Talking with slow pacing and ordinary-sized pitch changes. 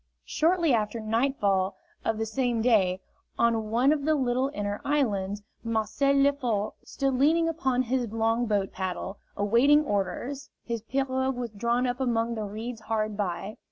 No: average, 155 wpm; average, 3.9 semitones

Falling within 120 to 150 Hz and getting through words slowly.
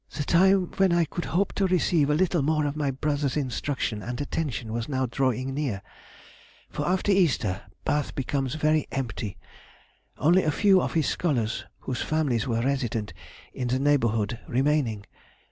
No: medium, 140 Hz; average, 160 wpm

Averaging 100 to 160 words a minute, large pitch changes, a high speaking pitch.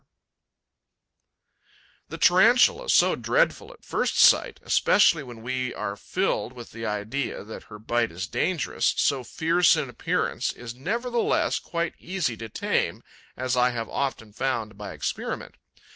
No: average, 140 wpm; wide, 7.2 semitones; low, 125 Hz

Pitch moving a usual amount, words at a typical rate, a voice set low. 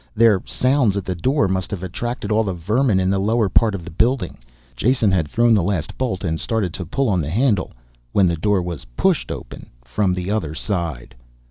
No: average, 4.2 semitones; fast, 215 wpm; very low, 95 Hz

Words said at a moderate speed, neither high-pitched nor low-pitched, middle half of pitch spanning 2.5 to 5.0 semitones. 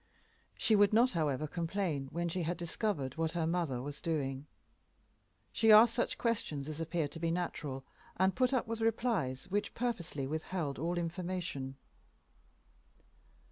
No: average, 145 wpm; medium, 170 Hz; wide, 5.5 semitones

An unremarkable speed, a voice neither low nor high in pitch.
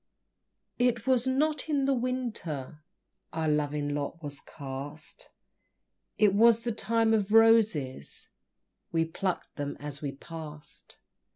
No: slow, 120 wpm; medium, 170 Hz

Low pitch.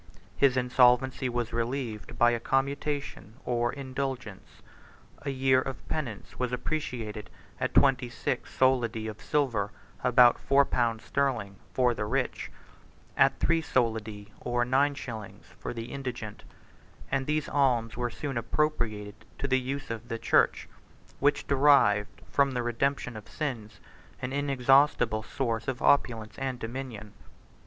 Yes: low, 125 Hz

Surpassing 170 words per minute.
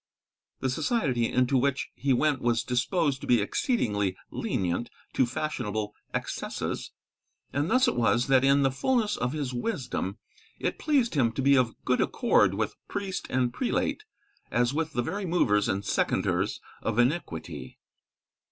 No: average, 150 wpm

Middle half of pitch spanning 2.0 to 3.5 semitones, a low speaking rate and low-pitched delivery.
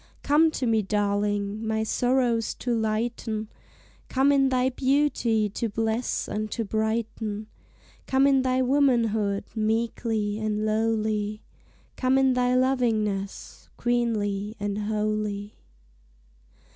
No: average, 2.9 semitones; slow, 110 wpm; high, 220 Hz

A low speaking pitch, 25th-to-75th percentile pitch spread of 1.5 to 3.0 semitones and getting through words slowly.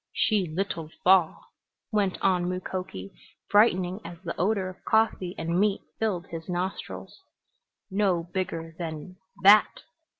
No: medium, 185 Hz; average, 2.7 semitones; slow, 125 wpm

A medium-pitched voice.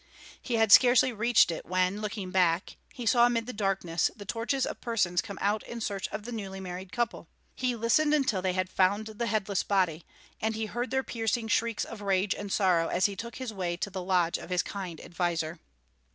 No: high, 205 Hz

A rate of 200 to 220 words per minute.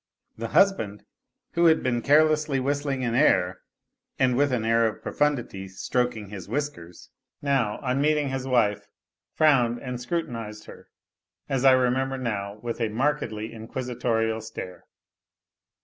No: slow, 135 wpm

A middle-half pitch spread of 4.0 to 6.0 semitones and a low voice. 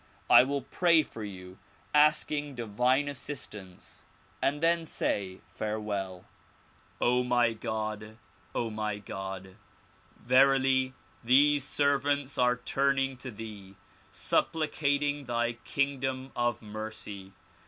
Yes: average, 4.7 semitones; low, 125 Hz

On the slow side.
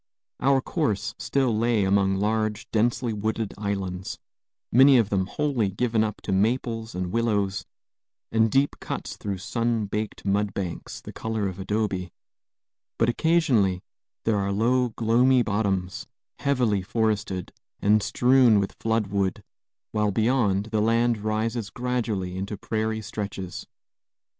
Yes: slow, 130 wpm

